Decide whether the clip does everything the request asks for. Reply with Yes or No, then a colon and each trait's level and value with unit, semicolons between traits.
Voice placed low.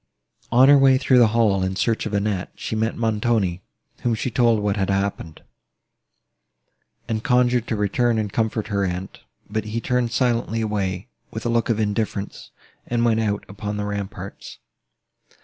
Yes: low, 110 Hz